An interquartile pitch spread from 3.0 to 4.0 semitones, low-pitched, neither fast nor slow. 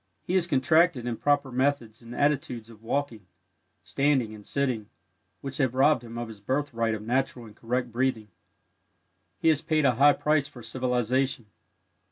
Yes: average, 3.6 semitones; low, 130 Hz; average, 160 wpm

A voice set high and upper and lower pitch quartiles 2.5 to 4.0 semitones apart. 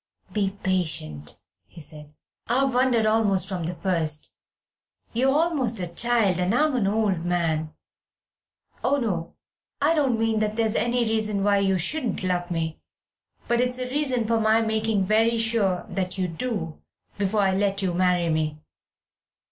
No: high, 205 Hz; average, 4.6 semitones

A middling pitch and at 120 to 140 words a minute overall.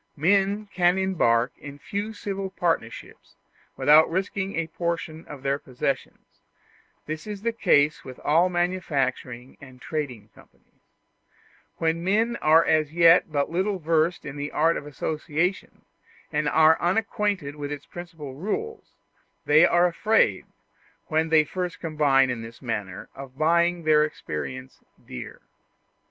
Yes: medium, 160 Hz; slow, 135 wpm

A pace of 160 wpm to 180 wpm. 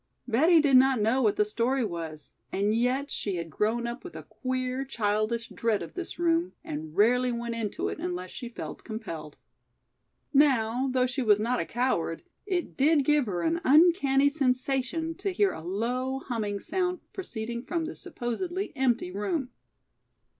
Yes: average, 170 wpm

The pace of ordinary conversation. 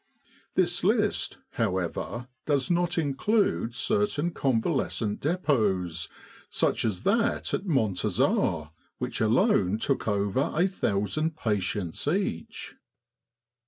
No: slow, 95 wpm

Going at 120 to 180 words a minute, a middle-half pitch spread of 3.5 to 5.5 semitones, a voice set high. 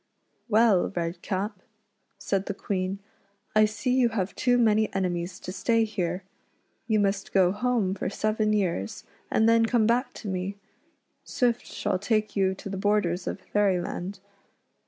No: average, 155 wpm; average, 2.8 semitones; high, 205 Hz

